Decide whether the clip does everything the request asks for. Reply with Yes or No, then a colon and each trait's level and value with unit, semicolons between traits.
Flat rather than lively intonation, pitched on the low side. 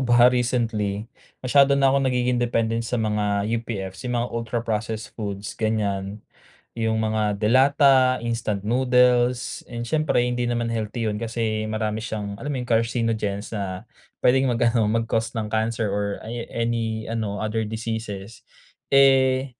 Yes: narrow, 2.3 semitones; low, 115 Hz